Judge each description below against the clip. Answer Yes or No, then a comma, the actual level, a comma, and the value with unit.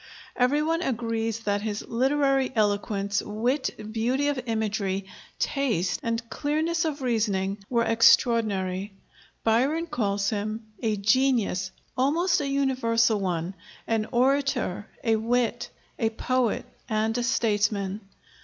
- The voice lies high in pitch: Yes, high, 230 Hz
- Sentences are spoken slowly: Yes, slow, 115 wpm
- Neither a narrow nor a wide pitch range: Yes, average, 4.2 semitones